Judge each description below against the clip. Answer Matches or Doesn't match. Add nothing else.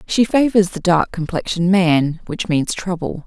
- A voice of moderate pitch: Matches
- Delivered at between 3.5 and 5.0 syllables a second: Matches